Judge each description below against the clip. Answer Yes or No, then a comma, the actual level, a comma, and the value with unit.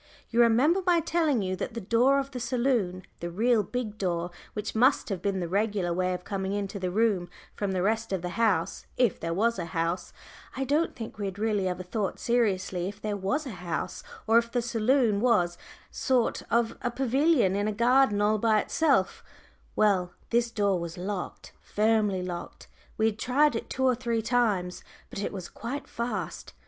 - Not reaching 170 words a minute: No, average, 200 wpm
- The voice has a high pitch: Yes, high, 215 Hz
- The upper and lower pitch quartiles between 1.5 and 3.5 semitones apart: No, average, 4.3 semitones